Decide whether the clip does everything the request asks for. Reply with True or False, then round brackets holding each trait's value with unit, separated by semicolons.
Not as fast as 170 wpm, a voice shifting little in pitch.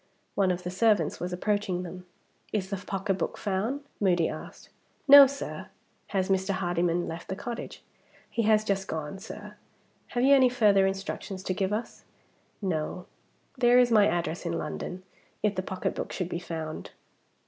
False (160 wpm; 3.0 semitones)